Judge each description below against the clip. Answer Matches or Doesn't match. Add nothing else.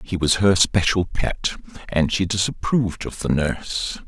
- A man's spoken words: Matches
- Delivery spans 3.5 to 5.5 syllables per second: Matches